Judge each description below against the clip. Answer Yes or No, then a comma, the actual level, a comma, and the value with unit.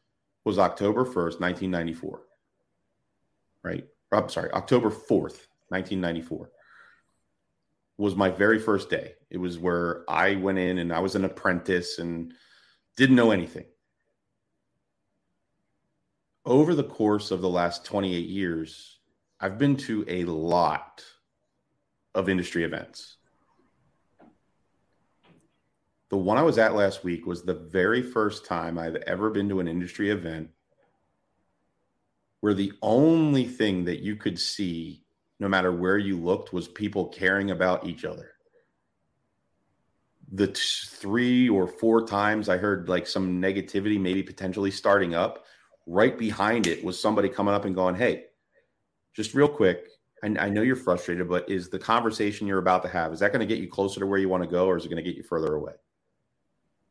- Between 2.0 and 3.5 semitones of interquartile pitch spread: Yes, average, 2.8 semitones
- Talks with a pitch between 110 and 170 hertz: No, very low, 95 Hz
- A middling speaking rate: Yes, average, 155 wpm